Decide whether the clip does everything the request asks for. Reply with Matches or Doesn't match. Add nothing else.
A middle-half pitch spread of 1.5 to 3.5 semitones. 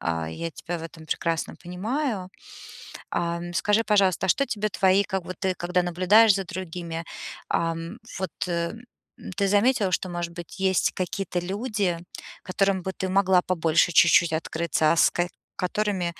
Matches